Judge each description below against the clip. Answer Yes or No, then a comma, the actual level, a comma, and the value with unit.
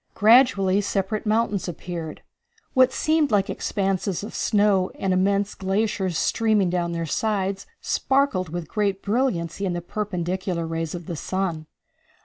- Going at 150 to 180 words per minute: No, slow, 135 wpm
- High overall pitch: Yes, high, 195 Hz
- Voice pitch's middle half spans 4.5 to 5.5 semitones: No, average, 3.2 semitones